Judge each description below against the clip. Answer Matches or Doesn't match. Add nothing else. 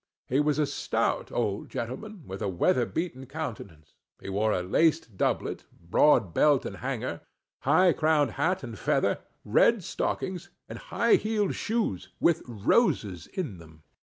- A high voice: Doesn't match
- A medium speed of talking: Matches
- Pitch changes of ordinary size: Doesn't match